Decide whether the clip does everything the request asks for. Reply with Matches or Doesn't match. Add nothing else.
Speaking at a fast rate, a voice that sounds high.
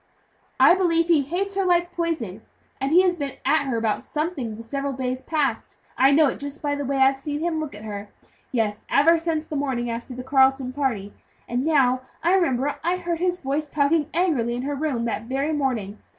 Matches